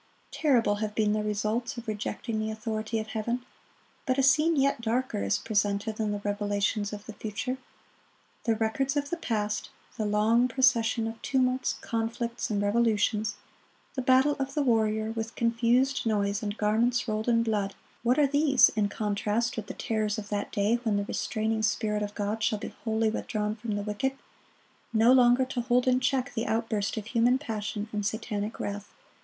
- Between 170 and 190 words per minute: Yes, average, 175 wpm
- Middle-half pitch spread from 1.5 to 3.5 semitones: Yes, narrow, 2.6 semitones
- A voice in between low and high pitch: No, high, 220 Hz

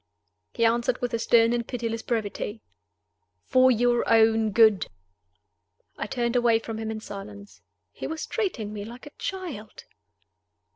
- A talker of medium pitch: No, high, 230 Hz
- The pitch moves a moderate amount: No, narrow, 1.8 semitones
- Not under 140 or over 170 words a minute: Yes, average, 145 wpm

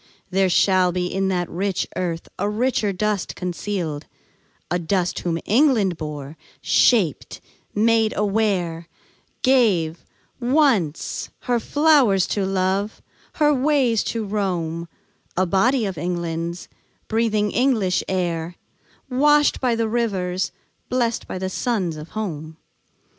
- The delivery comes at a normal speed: No, slow, 115 wpm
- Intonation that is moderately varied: Yes, average, 4.7 semitones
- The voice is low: No, high, 195 Hz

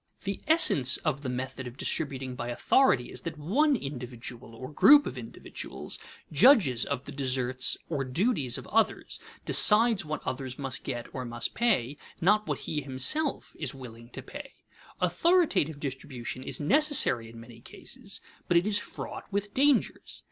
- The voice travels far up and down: Yes, wide, 8.8 semitones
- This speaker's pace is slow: No, average, 160 wpm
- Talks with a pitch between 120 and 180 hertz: Yes, medium, 140 Hz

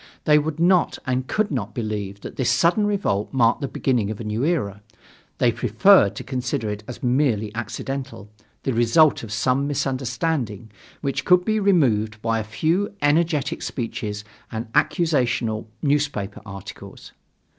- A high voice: No, low, 125 Hz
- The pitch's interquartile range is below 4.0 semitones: No, wide, 5.6 semitones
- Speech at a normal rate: Yes, average, 150 wpm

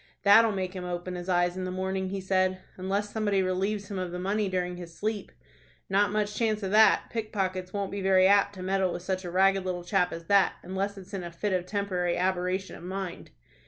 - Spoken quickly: Yes, fast, 225 wpm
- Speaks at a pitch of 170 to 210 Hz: Yes, high, 190 Hz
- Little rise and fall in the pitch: Yes, narrow, 1.7 semitones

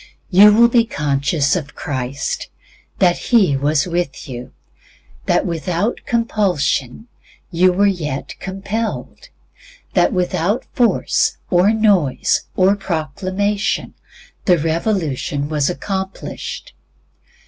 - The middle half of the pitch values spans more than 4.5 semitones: Yes, wide, 5.6 semitones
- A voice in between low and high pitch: Yes, medium, 180 Hz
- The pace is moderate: No, slow, 100 wpm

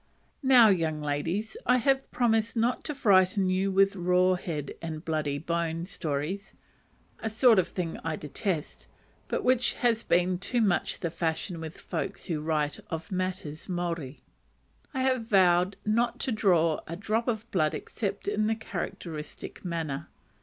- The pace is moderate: Yes, average, 155 wpm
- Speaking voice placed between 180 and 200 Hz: Yes, medium, 185 Hz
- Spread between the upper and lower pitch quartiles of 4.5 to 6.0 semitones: Yes, average, 5.2 semitones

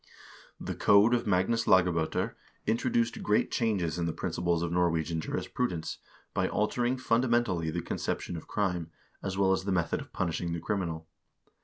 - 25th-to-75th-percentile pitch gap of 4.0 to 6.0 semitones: Yes, average, 4.7 semitones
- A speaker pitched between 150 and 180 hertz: No, very low, 90 Hz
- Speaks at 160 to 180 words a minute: Yes, average, 165 wpm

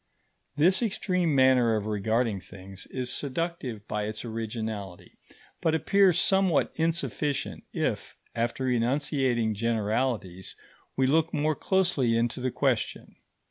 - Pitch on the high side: No, low, 125 Hz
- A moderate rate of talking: No, slow, 115 wpm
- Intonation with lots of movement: Yes, wide, 6.0 semitones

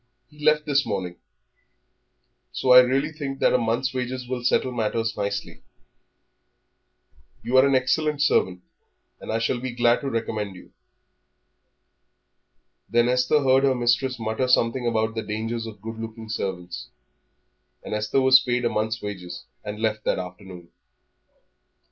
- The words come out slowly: No, average, 150 wpm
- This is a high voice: No, low, 120 Hz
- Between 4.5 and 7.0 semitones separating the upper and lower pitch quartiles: No, average, 3.1 semitones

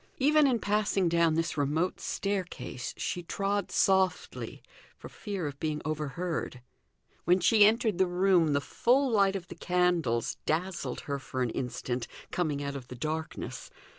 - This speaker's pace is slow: No, average, 155 wpm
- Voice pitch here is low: No, medium, 175 Hz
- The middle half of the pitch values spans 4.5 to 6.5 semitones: Yes, average, 5.2 semitones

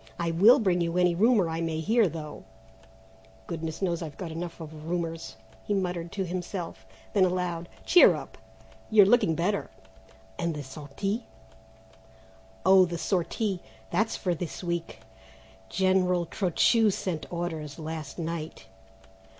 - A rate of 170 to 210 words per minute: No, slow, 135 wpm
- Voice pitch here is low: No, medium, 175 Hz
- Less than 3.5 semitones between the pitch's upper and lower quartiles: Yes, narrow, 2.6 semitones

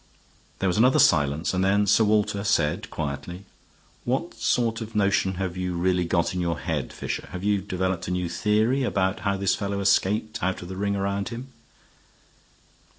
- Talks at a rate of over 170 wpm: Yes, average, 180 wpm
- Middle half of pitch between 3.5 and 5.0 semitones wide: No, narrow, 2.4 semitones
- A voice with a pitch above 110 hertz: No, very low, 95 Hz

